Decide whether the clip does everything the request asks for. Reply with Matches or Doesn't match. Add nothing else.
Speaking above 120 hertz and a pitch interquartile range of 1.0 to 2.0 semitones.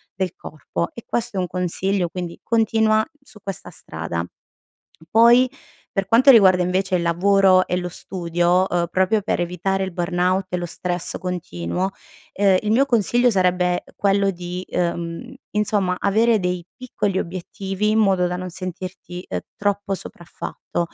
Doesn't match